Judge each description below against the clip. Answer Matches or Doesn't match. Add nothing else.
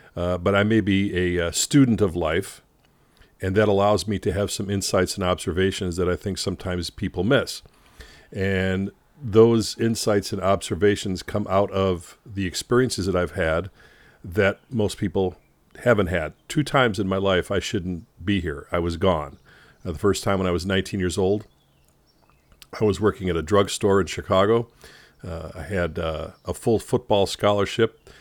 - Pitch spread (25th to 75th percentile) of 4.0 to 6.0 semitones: Doesn't match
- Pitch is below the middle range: Matches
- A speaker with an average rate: Matches